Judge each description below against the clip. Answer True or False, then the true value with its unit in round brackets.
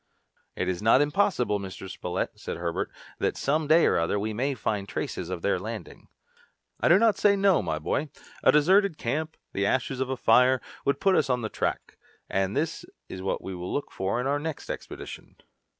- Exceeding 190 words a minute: True (200 wpm)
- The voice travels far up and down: True (7.7 semitones)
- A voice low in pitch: True (125 Hz)